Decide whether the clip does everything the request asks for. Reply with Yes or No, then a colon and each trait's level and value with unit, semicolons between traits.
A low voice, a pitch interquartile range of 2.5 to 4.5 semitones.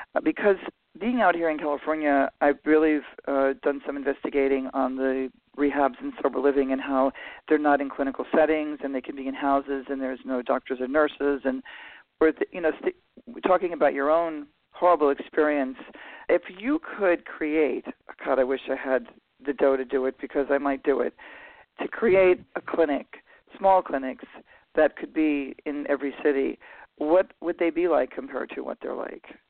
No: medium, 145 Hz; average, 2.8 semitones